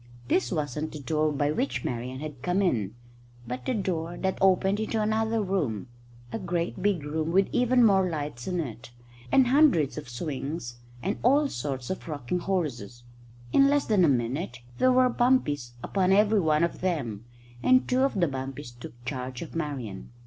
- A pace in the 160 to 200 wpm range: Yes, average, 180 wpm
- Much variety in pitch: Yes, wide, 7.1 semitones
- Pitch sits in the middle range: Yes, medium, 160 Hz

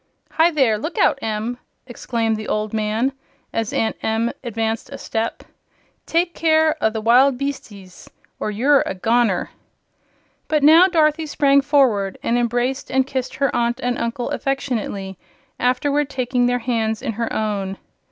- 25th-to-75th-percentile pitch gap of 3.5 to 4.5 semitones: Yes, average, 4.0 semitones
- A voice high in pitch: Yes, high, 245 Hz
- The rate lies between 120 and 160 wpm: Yes, average, 150 wpm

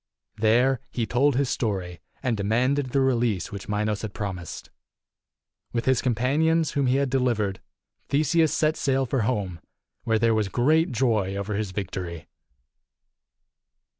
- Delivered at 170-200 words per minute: No, average, 140 wpm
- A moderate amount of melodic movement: Yes, average, 4.6 semitones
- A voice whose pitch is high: No, low, 120 Hz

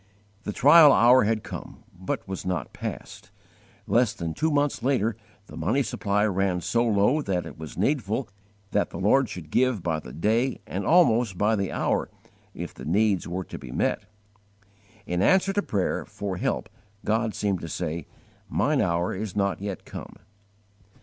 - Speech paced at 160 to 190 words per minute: Yes, average, 170 wpm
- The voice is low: Yes, low, 105 Hz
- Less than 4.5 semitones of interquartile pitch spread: No, average, 4.8 semitones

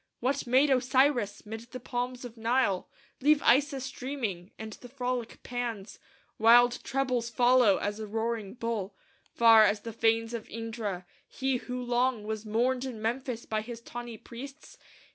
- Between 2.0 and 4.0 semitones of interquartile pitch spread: Yes, narrow, 2.5 semitones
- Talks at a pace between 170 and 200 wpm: No, average, 155 wpm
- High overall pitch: Yes, high, 235 Hz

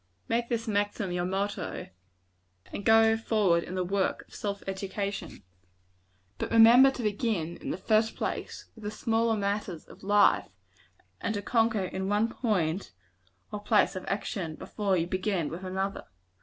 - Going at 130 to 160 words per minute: Yes, average, 155 wpm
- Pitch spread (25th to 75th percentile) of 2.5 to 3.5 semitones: Yes, average, 2.8 semitones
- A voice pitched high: Yes, high, 205 Hz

